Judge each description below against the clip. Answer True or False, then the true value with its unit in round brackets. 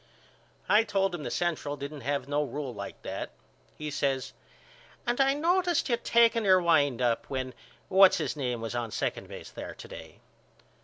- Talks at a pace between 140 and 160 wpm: False (175 wpm)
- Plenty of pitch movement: True (7.6 semitones)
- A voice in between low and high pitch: True (150 Hz)